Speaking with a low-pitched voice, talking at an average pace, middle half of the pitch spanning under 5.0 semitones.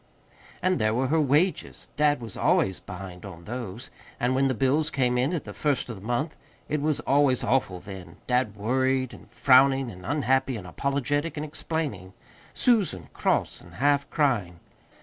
No: low, 130 Hz; average, 170 wpm; wide, 5.4 semitones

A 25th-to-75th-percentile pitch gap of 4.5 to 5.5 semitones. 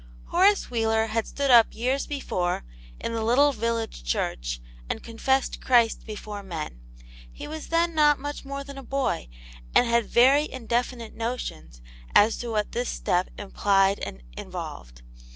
Yes: average, 4.9 semitones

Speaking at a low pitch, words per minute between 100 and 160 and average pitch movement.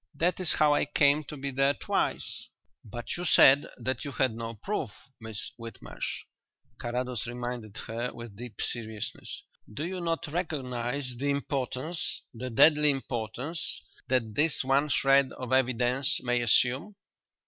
Yes: low, 130 Hz; average, 145 wpm; average, 3.3 semitones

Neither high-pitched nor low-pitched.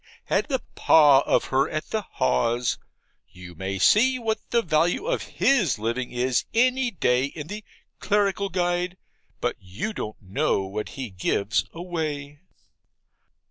Yes: medium, 150 Hz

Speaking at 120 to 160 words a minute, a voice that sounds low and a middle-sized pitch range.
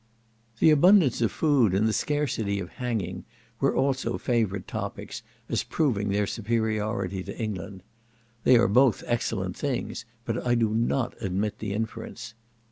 Yes: average, 145 wpm; low, 115 Hz; average, 3.7 semitones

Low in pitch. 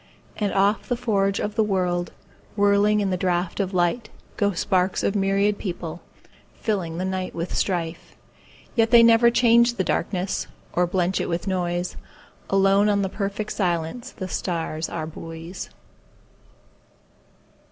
No: high, 190 Hz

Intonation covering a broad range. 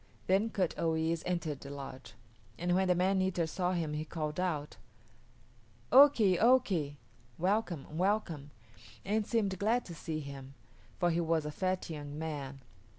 No: average, 4.0 semitones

